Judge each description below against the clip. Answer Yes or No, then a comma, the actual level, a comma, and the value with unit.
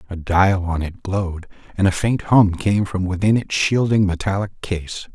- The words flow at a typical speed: Yes, average, 185 wpm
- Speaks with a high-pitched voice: No, very low, 95 Hz